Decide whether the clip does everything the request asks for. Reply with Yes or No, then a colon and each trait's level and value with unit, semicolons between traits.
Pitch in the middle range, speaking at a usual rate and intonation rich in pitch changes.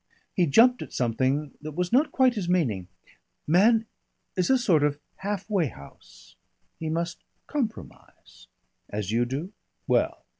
Yes: medium, 170 Hz; average, 145 wpm; wide, 7.4 semitones